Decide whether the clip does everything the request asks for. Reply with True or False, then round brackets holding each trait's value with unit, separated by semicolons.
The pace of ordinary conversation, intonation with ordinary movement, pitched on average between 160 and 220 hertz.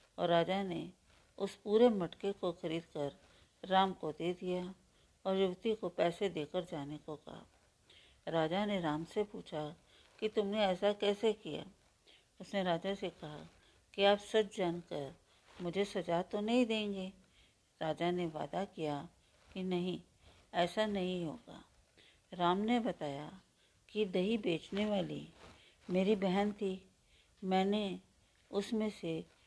True (135 wpm; 3.6 semitones; 185 Hz)